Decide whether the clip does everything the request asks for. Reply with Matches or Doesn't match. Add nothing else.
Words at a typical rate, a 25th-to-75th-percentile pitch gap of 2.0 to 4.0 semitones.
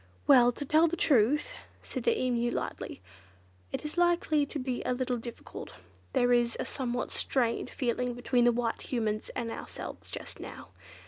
Matches